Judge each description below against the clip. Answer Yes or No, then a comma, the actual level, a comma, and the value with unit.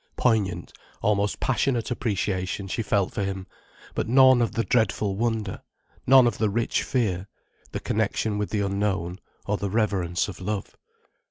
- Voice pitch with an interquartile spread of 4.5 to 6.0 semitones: No, average, 3.0 semitones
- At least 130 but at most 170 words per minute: Yes, average, 155 wpm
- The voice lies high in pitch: No, low, 105 Hz